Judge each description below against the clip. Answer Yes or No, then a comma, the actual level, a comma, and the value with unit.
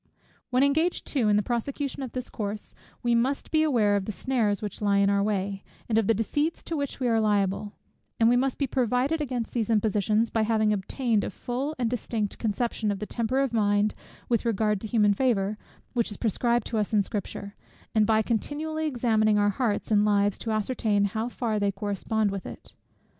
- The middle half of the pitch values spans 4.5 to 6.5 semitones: No, average, 3.3 semitones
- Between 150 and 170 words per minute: No, fast, 205 wpm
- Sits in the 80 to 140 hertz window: No, high, 220 Hz